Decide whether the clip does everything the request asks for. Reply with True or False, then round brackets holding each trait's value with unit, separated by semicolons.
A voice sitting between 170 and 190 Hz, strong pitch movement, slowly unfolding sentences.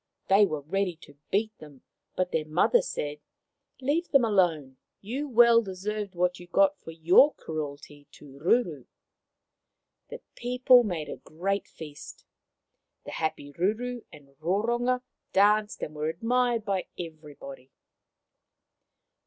True (185 Hz; 6.9 semitones; 130 wpm)